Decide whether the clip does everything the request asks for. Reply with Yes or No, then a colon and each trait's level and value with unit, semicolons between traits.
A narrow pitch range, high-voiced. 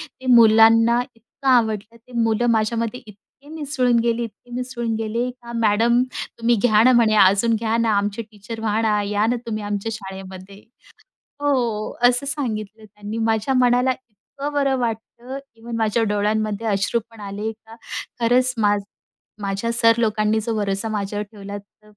Yes: narrow, 2.2 semitones; high, 225 Hz